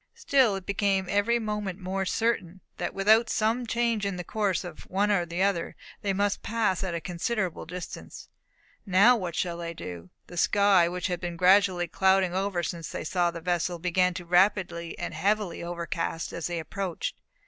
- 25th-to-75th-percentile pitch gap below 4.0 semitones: Yes, average, 2.8 semitones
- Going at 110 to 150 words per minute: No, average, 185 wpm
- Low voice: No, medium, 185 Hz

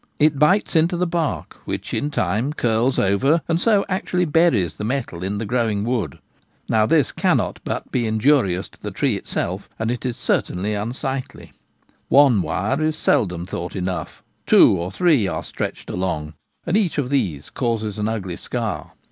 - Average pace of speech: Yes, average, 175 wpm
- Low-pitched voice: Yes, low, 115 Hz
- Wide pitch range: Yes, wide, 7.6 semitones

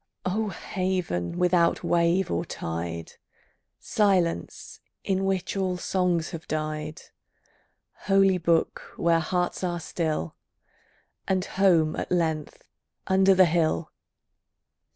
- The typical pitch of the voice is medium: Yes, medium, 175 Hz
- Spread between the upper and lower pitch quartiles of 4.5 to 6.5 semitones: No, average, 2.9 semitones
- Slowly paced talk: Yes, slow, 105 wpm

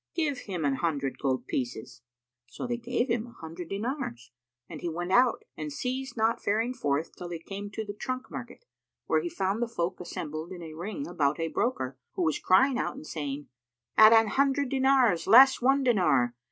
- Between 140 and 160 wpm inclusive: No, average, 195 wpm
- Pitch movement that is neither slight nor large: No, wide, 8.0 semitones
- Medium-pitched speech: No, high, 205 Hz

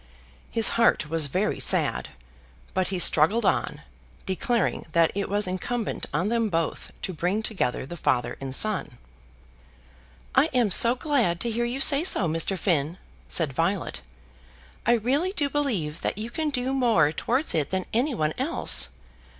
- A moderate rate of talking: Yes, average, 160 wpm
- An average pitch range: No, wide, 6.6 semitones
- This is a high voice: Yes, high, 205 Hz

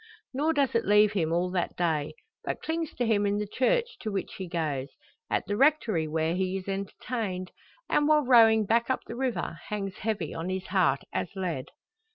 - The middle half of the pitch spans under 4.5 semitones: No, average, 5.0 semitones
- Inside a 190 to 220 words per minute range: Yes, average, 200 wpm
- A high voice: Yes, high, 200 Hz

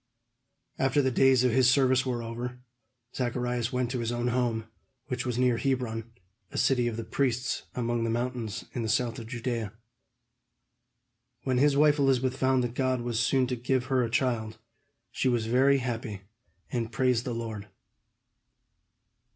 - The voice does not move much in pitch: Yes, narrow, 1.9 semitones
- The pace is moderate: Yes, average, 165 wpm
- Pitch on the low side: Yes, low, 125 Hz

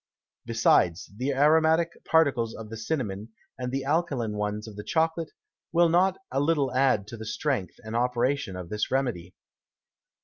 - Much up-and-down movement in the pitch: Yes, wide, 6.0 semitones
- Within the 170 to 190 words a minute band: No, average, 160 wpm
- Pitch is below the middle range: Yes, low, 125 Hz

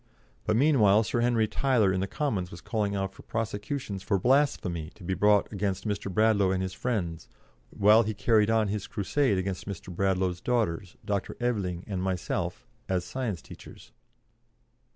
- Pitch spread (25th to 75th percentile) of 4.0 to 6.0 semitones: No, average, 3.2 semitones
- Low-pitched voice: Yes, low, 100 Hz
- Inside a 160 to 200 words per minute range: Yes, average, 165 wpm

